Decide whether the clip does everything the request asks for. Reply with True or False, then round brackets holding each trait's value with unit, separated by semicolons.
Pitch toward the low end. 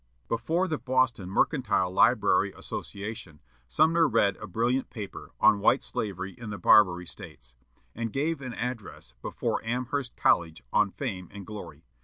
True (110 Hz)